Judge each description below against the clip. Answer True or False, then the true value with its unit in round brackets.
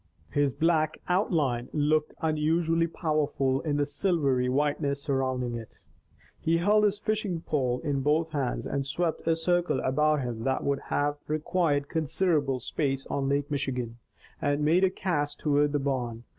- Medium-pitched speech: True (145 Hz)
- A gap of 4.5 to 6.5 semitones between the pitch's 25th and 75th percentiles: False (3.2 semitones)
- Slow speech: False (155 wpm)